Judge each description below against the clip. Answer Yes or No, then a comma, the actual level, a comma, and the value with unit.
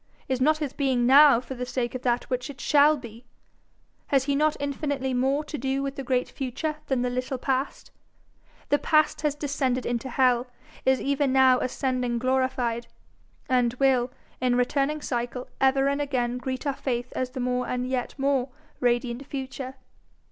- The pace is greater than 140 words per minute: Yes, average, 175 wpm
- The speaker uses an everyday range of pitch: No, narrow, 1.9 semitones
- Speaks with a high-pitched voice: Yes, very high, 260 Hz